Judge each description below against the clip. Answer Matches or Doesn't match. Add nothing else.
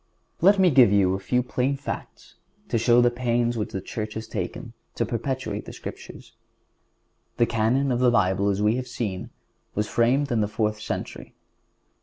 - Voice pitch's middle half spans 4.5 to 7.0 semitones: Doesn't match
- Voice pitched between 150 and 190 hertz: Doesn't match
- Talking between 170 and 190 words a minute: Matches